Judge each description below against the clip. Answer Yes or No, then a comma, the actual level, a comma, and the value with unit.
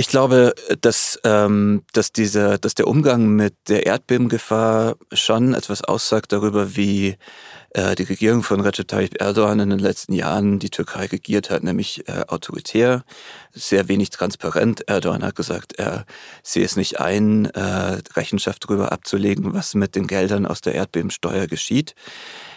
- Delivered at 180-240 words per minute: No, average, 145 wpm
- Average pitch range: No, narrow, 2.1 semitones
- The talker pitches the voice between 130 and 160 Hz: No, low, 105 Hz